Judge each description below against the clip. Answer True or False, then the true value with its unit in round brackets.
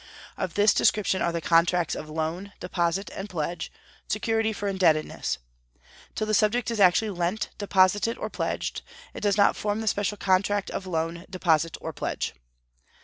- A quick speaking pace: False (160 wpm)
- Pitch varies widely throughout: False (3.3 semitones)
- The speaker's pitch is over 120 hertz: True (190 Hz)